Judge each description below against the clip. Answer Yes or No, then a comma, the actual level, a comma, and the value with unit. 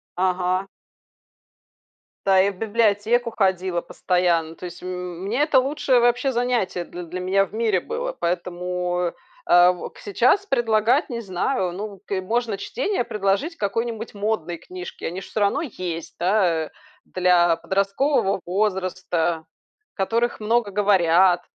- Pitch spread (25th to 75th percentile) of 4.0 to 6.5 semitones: Yes, average, 4.3 semitones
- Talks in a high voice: Yes, high, 195 Hz